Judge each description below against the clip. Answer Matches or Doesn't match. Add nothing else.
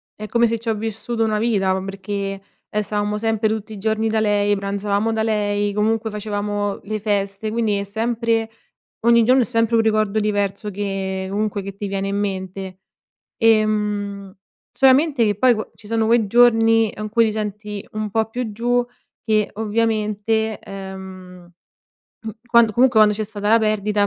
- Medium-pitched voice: Doesn't match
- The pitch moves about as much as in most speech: Doesn't match